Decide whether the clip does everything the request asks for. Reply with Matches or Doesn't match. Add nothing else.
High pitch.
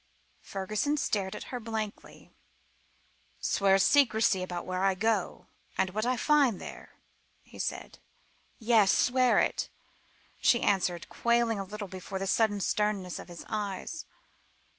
Matches